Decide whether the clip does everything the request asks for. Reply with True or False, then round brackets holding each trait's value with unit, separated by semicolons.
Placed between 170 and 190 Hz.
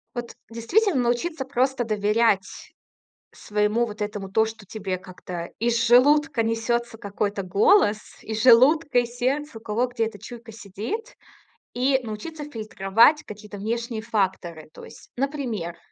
False (225 Hz)